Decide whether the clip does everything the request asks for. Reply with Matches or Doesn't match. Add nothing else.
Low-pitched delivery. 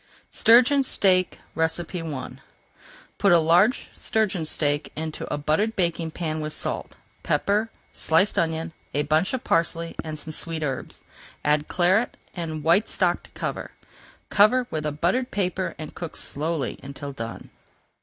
Doesn't match